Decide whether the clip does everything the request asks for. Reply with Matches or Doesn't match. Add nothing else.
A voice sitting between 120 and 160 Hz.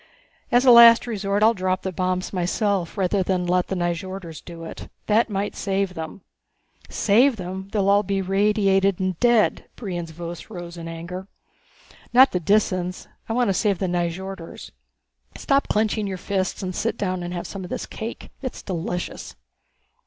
Doesn't match